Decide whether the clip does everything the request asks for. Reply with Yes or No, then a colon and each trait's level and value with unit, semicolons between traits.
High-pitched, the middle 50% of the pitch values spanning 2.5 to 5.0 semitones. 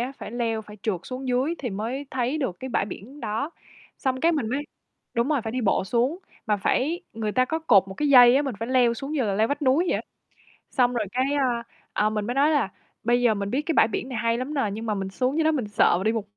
Yes: high, 245 Hz; average, 3.9 semitones